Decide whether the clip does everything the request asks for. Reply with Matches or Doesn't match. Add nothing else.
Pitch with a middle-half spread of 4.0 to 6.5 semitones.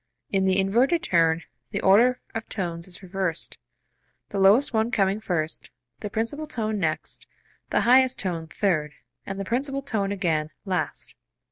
Matches